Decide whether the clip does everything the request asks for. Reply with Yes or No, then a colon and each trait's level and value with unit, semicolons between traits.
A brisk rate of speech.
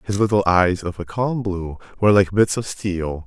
Yes: fast, 220 wpm